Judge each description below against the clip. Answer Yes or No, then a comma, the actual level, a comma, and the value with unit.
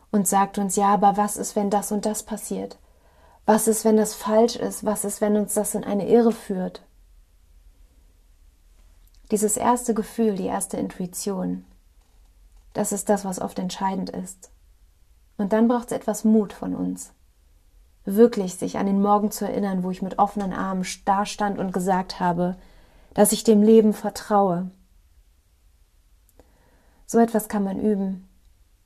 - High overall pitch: Yes, high, 195 Hz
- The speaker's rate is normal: Yes, average, 155 wpm